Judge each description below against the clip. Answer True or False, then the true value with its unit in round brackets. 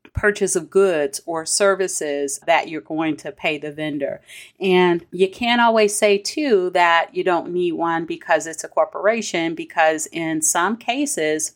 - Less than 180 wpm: True (160 wpm)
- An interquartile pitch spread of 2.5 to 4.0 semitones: True (3.5 semitones)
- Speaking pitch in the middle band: True (170 Hz)